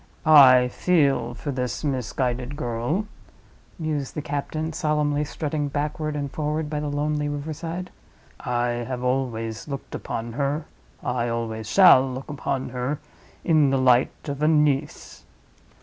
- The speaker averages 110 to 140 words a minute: Yes, slow, 135 wpm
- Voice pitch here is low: No, medium, 145 Hz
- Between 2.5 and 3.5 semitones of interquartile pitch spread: Yes, average, 3.2 semitones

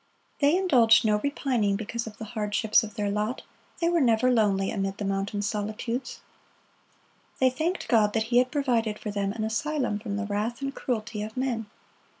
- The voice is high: Yes, high, 220 Hz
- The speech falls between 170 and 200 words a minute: Yes, average, 180 wpm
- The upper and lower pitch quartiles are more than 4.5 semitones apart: No, average, 3.3 semitones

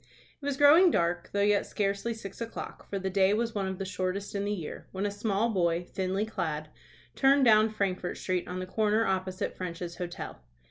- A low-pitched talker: No, high, 195 Hz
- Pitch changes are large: No, average, 2.8 semitones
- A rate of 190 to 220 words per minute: Yes, average, 200 wpm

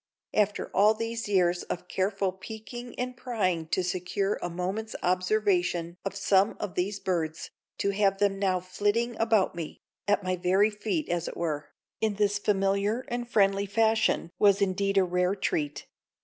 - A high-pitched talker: Yes, high, 195 Hz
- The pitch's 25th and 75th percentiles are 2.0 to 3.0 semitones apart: Yes, average, 2.7 semitones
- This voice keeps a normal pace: Yes, average, 165 wpm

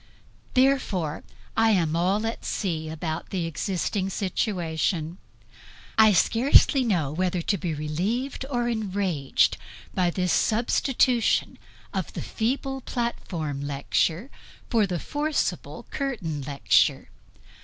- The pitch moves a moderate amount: No, wide, 6.3 semitones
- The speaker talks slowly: Yes, slow, 110 wpm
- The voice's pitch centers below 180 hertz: No, high, 190 Hz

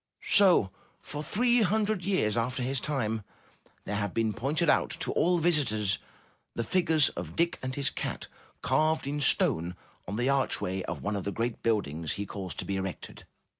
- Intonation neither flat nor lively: No, wide, 7.4 semitones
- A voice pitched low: Yes, low, 125 Hz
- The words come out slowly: No, average, 175 wpm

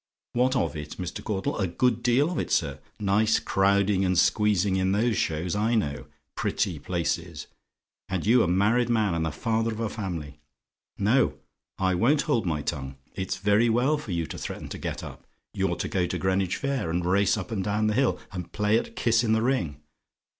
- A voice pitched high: No, low, 100 Hz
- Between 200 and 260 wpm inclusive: Yes, fast, 205 wpm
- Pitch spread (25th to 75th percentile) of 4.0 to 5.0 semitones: Yes, average, 4.4 semitones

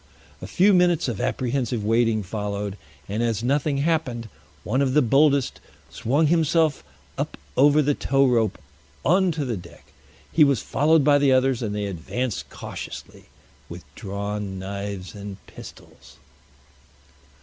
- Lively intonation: Yes, wide, 5.9 semitones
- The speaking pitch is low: Yes, low, 125 Hz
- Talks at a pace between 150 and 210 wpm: No, average, 140 wpm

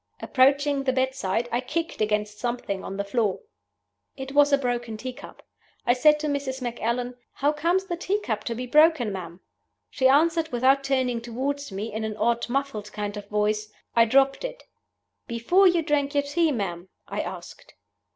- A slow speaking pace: No, average, 180 wpm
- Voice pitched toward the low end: No, very high, 255 Hz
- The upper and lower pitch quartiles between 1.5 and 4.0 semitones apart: No, average, 4.6 semitones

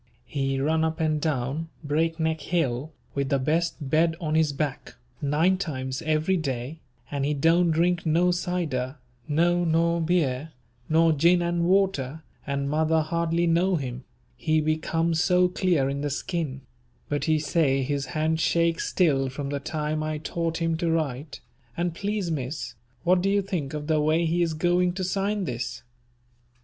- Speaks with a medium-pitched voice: Yes, medium, 160 Hz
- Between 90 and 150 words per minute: No, average, 170 wpm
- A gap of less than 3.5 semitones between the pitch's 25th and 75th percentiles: Yes, average, 3.0 semitones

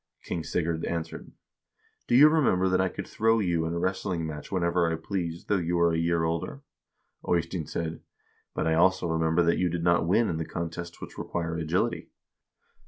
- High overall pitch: No, very low, 85 Hz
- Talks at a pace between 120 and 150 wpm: No, fast, 205 wpm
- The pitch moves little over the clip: Yes, narrow, 2.0 semitones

